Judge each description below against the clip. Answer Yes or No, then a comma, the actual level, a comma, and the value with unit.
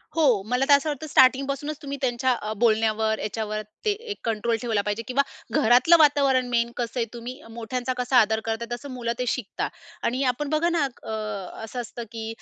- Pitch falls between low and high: No, high, 245 Hz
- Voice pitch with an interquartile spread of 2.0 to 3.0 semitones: No, average, 3.6 semitones